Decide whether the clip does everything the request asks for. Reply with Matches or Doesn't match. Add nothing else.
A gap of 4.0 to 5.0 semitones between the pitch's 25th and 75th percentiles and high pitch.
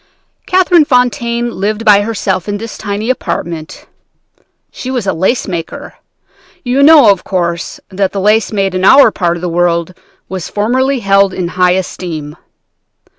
Matches